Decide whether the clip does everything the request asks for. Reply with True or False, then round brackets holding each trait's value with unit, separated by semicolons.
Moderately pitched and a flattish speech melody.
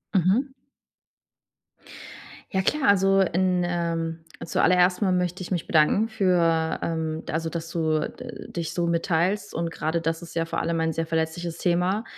True (170 Hz; 2.3 semitones)